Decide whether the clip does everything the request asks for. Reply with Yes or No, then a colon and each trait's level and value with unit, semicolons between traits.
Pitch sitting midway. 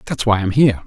No: low, 110 Hz